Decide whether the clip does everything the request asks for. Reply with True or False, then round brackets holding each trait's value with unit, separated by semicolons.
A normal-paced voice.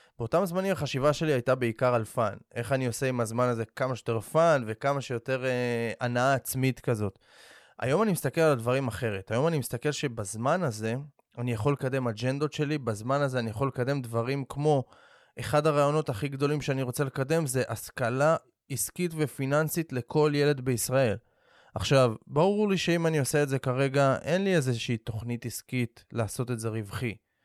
False (170 wpm)